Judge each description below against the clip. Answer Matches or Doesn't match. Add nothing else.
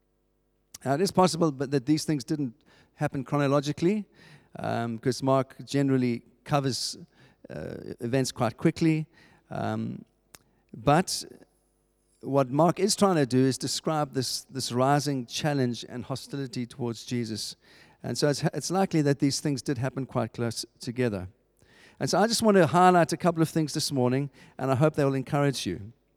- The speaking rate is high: Doesn't match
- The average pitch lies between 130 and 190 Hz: Matches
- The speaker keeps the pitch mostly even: Doesn't match